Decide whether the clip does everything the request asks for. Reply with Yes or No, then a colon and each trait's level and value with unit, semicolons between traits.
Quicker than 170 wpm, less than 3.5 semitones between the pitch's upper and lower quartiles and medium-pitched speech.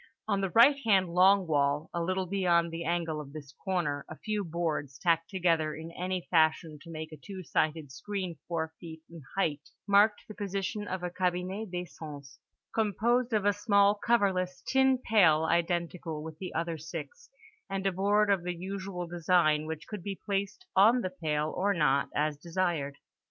No: average, 180 wpm; average, 3.8 semitones; medium, 175 Hz